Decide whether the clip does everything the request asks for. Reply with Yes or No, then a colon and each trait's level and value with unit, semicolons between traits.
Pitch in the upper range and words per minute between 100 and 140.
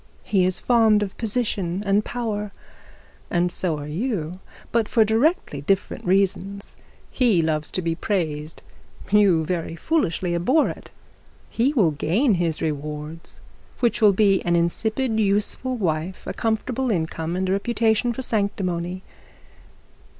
Yes: high, 195 Hz; slow, 135 wpm